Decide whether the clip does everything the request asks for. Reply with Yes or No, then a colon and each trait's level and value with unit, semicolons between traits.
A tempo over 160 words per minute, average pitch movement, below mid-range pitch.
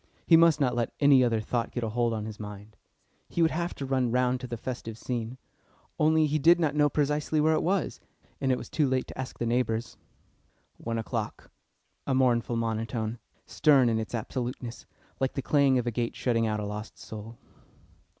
Yes: average, 200 wpm; average, 3.8 semitones; low, 125 Hz